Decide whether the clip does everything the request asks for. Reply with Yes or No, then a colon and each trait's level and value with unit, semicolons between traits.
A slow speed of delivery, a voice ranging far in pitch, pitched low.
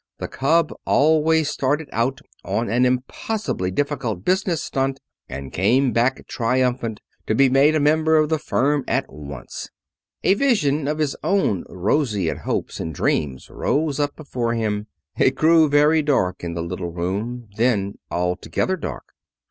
No: average, 150 wpm; wide, 6.5 semitones; low, 130 Hz